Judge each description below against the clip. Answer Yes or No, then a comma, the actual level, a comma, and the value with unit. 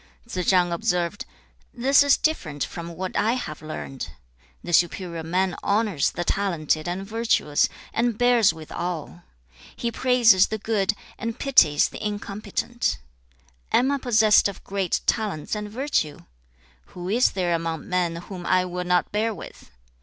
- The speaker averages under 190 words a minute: Yes, average, 155 wpm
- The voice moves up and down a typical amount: Yes, average, 4.7 semitones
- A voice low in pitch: No, high, 190 Hz